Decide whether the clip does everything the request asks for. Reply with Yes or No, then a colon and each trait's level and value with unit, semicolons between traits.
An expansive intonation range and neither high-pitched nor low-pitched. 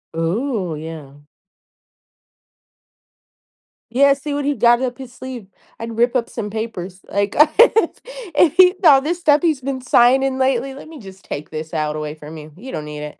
No: wide, 8.6 semitones; high, 240 Hz